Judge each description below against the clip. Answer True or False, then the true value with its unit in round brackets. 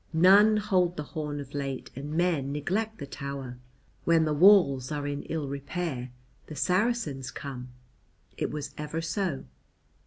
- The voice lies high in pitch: False (150 Hz)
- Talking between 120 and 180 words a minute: True (150 wpm)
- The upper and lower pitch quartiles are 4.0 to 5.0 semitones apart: True (4.4 semitones)